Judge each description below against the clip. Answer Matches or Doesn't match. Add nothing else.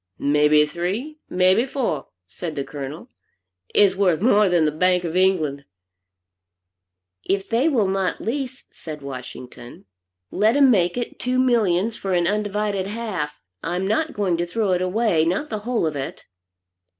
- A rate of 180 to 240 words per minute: Doesn't match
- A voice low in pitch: Doesn't match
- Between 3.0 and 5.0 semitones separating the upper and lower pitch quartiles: Doesn't match